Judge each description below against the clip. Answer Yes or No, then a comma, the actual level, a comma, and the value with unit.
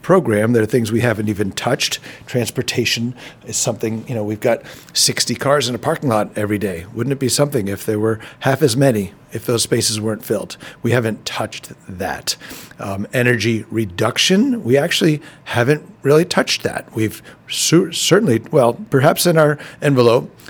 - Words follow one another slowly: No, average, 175 wpm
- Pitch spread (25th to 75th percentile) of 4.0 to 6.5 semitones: Yes, average, 4.7 semitones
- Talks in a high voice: No, low, 120 Hz